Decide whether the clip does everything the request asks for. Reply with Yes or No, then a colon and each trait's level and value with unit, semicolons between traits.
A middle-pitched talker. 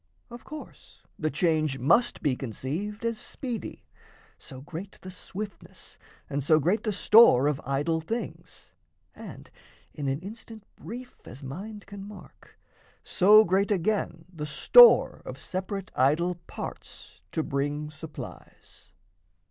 Yes: medium, 175 Hz